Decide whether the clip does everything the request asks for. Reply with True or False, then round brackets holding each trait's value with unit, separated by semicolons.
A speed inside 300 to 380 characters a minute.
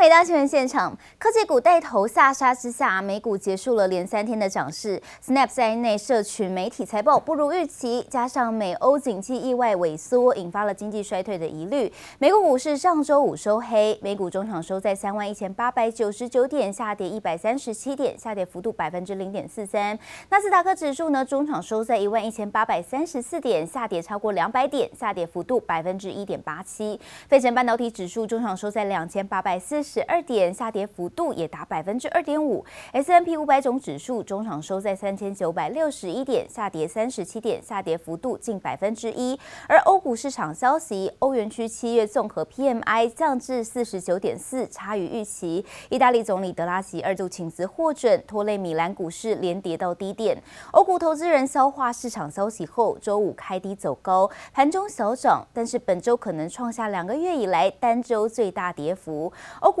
True (310 characters per minute)